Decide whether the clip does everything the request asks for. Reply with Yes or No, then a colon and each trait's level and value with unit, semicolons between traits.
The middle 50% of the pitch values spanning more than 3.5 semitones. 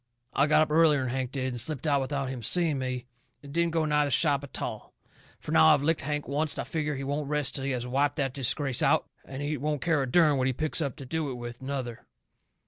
No: narrow, 2.5 semitones